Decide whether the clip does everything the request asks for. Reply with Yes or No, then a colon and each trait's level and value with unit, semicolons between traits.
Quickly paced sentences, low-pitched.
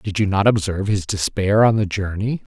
Yes: fast, 210 wpm; low, 100 Hz